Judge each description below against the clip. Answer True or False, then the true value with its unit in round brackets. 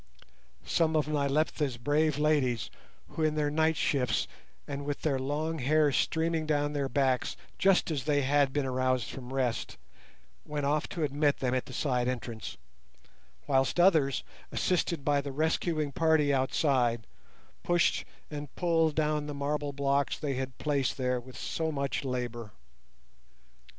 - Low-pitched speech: False (145 Hz)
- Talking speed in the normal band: True (150 wpm)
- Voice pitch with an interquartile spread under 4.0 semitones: True (2.7 semitones)